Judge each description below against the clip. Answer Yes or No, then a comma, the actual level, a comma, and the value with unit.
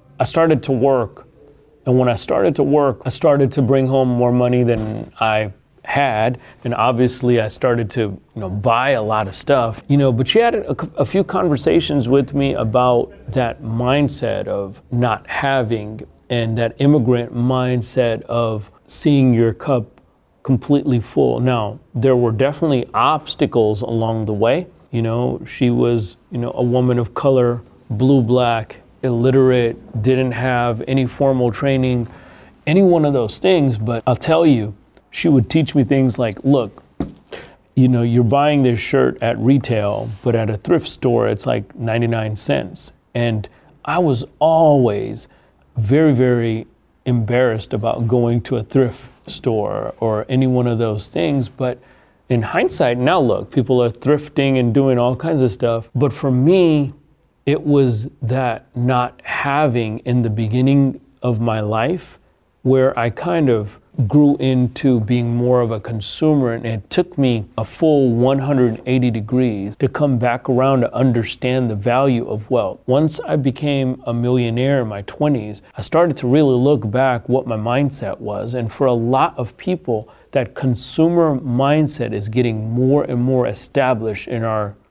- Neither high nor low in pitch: No, low, 125 Hz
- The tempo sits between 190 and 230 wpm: No, average, 160 wpm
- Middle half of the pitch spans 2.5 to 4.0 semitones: Yes, average, 2.8 semitones